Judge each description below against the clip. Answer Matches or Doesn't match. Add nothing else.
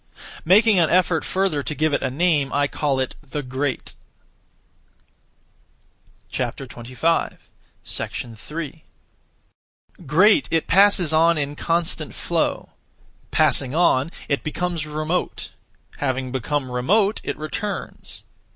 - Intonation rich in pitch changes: Doesn't match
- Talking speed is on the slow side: Matches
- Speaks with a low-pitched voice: Doesn't match